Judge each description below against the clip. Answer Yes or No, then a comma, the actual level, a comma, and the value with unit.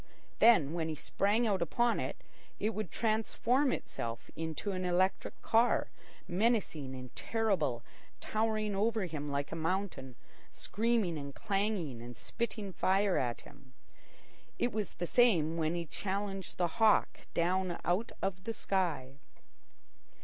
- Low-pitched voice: No, high, 190 Hz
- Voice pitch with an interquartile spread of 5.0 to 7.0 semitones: Yes, wide, 5.4 semitones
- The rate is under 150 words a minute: Yes, slow, 135 wpm